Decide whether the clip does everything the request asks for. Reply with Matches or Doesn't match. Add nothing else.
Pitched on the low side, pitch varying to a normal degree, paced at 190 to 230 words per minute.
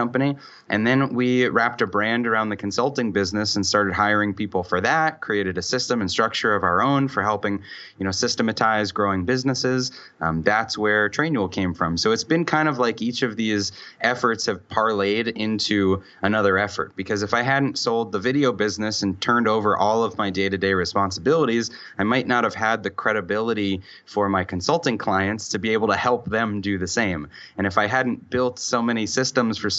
Matches